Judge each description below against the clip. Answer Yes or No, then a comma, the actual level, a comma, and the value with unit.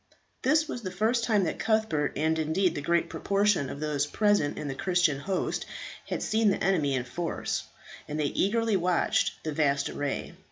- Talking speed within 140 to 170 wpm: No, average, 185 wpm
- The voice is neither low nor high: Yes, medium, 175 Hz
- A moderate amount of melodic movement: No, wide, 5.8 semitones